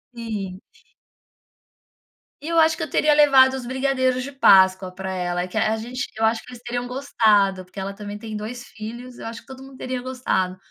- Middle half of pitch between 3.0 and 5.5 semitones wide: Yes, average, 4.8 semitones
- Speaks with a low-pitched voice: No, high, 235 Hz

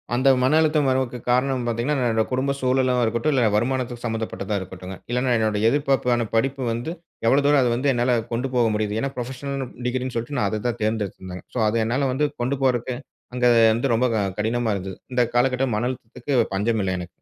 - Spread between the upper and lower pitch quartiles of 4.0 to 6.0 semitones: No, average, 2.9 semitones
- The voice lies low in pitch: Yes, low, 125 Hz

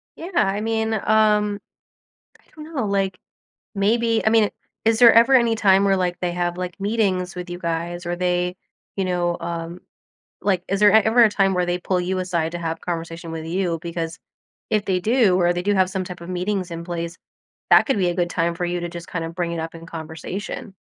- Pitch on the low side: No, medium, 180 Hz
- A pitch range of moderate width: Yes, average, 3.0 semitones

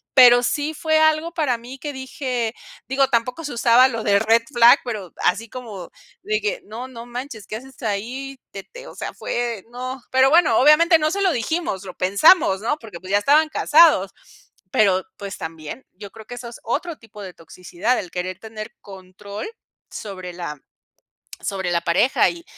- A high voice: Yes, high, 235 Hz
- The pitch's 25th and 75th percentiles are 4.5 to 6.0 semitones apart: Yes, wide, 5.6 semitones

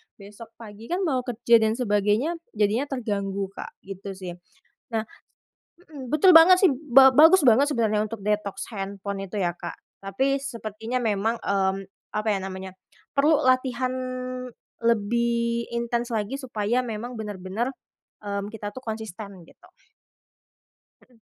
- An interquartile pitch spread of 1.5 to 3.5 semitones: No, average, 4.0 semitones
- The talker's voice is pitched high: Yes, high, 225 Hz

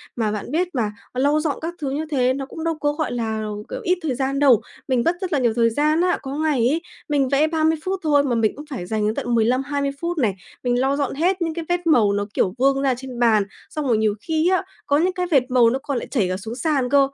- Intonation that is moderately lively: Yes, average, 4.6 semitones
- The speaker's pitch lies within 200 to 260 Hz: No, very high, 275 Hz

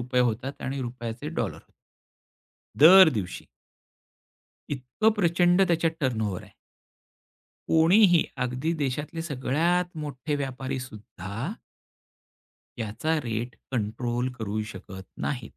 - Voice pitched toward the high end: No, low, 130 Hz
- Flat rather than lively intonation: No, wide, 5.5 semitones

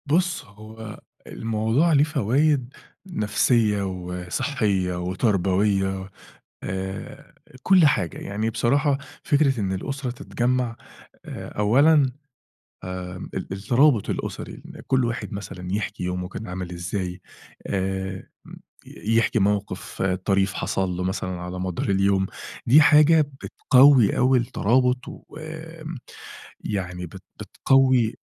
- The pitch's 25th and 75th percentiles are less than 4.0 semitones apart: No, wide, 5.6 semitones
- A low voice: Yes, low, 105 Hz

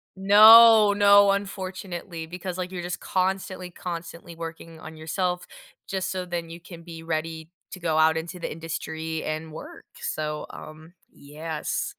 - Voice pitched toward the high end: No, medium, 170 Hz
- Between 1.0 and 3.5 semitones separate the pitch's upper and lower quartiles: Yes, average, 2.7 semitones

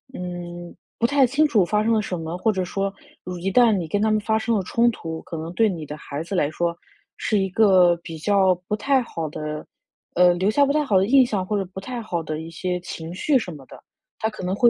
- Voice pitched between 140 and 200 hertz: Yes, high, 190 Hz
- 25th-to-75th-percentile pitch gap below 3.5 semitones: No, average, 4.3 semitones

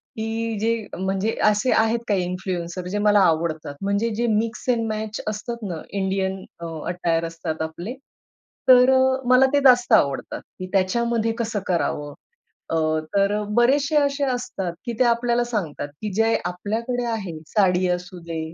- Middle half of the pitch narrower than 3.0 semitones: No, average, 4.8 semitones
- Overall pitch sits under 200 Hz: No, high, 210 Hz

